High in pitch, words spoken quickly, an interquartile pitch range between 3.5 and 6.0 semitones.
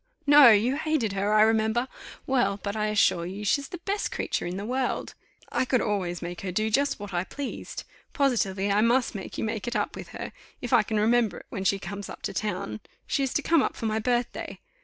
Yes: high, 220 Hz; fast, 230 wpm; average, 4.1 semitones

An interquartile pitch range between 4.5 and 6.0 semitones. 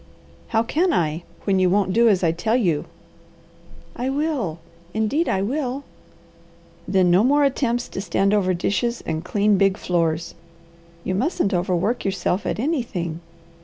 Yes: average, 5.3 semitones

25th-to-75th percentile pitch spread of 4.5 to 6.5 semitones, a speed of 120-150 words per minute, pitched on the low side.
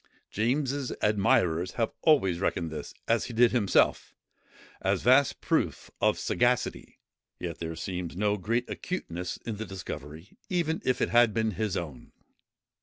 Yes: wide, 5.6 semitones; average, 145 wpm; low, 105 Hz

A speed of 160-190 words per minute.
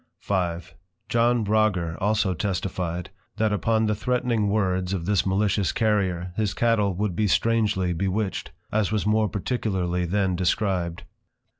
No: slow, 135 wpm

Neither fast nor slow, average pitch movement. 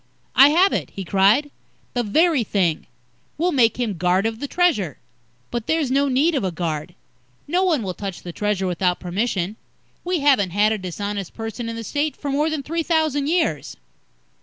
No: average, 185 wpm; wide, 7.5 semitones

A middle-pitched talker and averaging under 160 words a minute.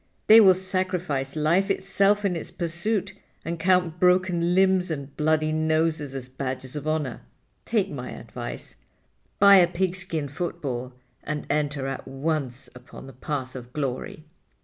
Yes: medium, 155 Hz; average, 145 wpm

